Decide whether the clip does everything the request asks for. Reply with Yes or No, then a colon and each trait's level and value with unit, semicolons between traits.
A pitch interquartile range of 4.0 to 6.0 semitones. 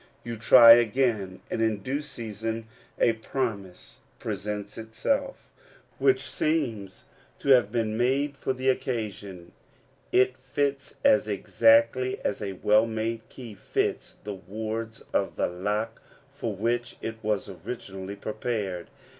No: average, 3.3 semitones